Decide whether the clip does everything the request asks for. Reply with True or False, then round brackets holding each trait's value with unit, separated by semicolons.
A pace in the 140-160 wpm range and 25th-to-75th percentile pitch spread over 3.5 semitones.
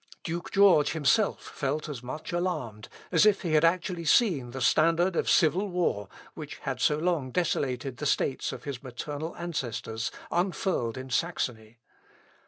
True (155 wpm; 5.1 semitones)